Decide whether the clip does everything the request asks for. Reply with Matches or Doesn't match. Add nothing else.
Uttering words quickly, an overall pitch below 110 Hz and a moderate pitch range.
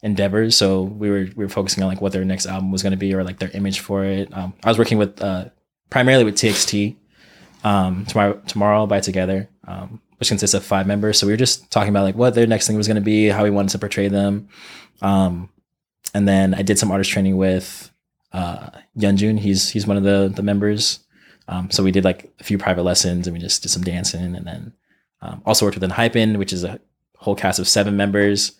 Doesn't match